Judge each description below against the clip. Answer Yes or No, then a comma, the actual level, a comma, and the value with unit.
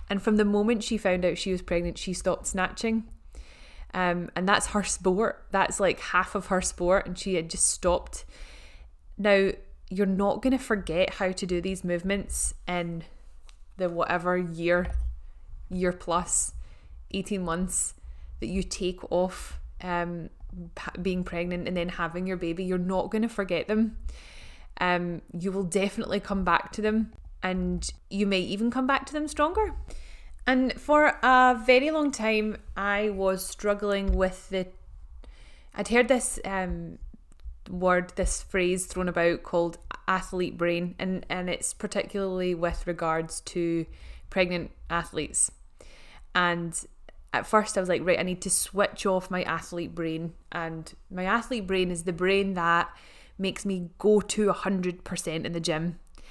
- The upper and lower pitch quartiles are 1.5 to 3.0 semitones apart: Yes, narrow, 2.6 semitones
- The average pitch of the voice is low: No, medium, 185 Hz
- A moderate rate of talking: Yes, average, 160 wpm